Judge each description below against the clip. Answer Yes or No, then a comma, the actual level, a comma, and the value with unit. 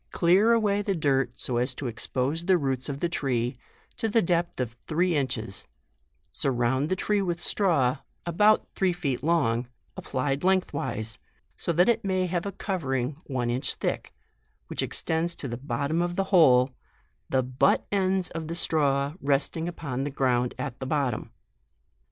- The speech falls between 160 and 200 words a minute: Yes, average, 170 wpm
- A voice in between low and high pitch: Yes, medium, 145 Hz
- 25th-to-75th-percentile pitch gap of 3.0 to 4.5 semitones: No, wide, 5.4 semitones